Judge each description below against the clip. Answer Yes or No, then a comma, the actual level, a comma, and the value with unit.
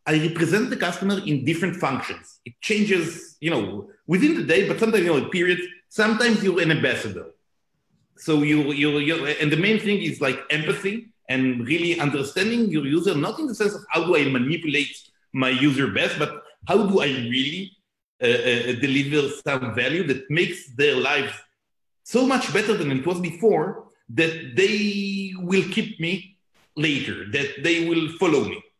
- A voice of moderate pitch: Yes, medium, 170 Hz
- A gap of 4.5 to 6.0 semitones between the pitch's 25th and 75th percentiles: Yes, average, 5.2 semitones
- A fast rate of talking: No, average, 175 wpm